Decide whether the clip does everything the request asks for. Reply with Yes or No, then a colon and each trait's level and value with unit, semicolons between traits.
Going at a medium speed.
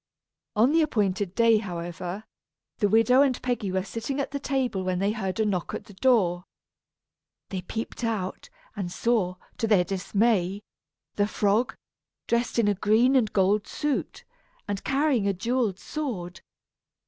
Yes: average, 155 wpm